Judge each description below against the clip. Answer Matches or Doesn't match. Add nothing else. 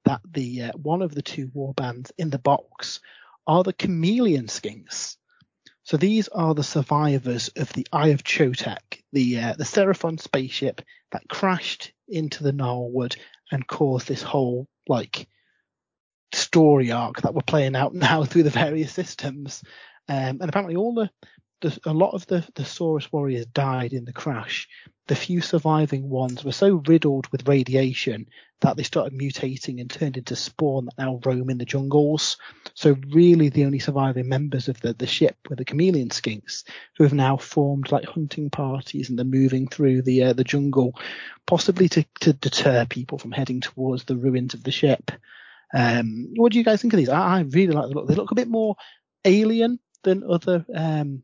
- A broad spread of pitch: Doesn't match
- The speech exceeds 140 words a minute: Matches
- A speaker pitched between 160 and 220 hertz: Doesn't match